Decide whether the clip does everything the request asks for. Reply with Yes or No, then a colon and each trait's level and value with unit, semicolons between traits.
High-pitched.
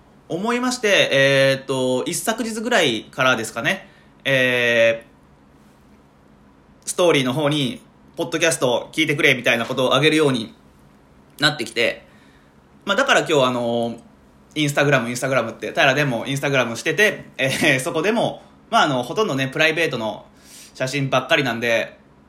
No: low, 125 Hz